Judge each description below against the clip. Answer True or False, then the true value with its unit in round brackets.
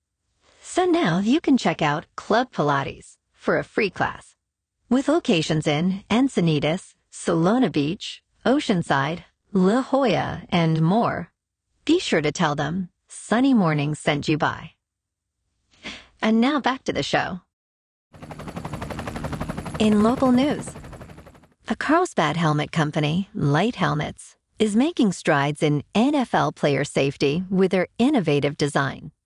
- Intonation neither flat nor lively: False (8.2 semitones)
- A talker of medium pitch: True (180 Hz)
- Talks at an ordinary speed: False (120 wpm)